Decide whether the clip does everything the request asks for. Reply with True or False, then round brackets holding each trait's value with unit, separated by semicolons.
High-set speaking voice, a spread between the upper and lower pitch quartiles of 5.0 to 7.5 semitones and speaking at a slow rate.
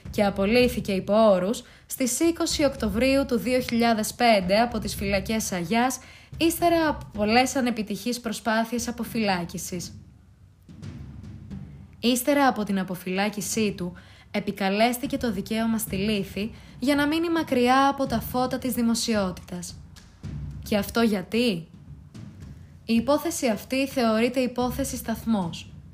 False (225 Hz; 4.2 semitones; 105 wpm)